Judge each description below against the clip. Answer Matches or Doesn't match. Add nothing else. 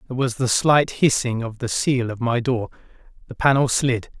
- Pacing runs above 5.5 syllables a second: Doesn't match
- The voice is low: Matches